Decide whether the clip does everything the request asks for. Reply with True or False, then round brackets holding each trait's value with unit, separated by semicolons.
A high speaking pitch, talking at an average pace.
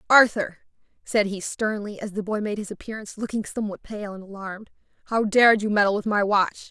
True (210 Hz; 195 wpm)